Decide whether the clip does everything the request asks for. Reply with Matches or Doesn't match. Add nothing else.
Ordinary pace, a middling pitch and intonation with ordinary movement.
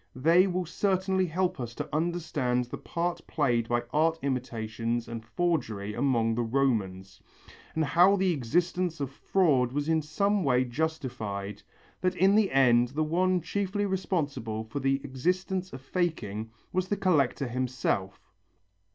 Doesn't match